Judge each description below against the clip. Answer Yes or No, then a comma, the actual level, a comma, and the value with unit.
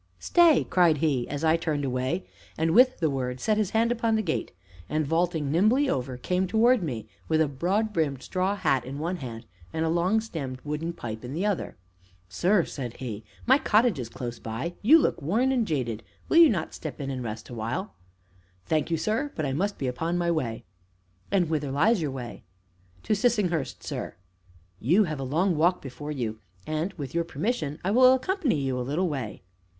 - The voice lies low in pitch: No, medium, 160 Hz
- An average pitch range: No, wide, 7.1 semitones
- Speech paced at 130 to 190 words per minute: No, average, 200 wpm